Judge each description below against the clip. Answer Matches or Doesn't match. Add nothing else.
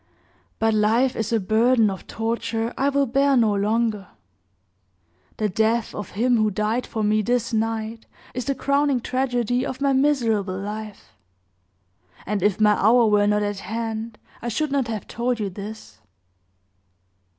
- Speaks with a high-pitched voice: Matches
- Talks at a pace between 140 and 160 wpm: Matches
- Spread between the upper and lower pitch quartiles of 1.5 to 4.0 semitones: Matches